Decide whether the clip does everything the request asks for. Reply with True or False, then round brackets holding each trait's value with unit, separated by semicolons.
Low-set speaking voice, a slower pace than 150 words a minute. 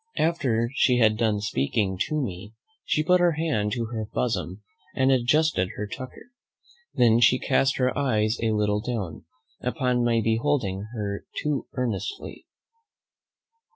True (120 Hz; 140 wpm)